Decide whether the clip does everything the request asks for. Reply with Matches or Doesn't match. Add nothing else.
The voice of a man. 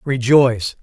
Matches